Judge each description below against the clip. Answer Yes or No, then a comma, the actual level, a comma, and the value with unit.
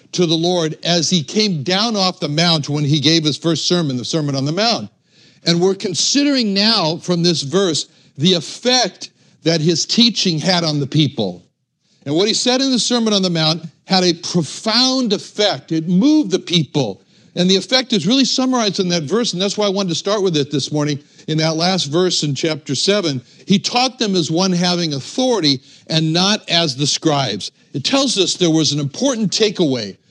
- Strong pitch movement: No, average, 4.7 semitones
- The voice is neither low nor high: Yes, medium, 175 Hz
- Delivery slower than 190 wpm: No, fast, 205 wpm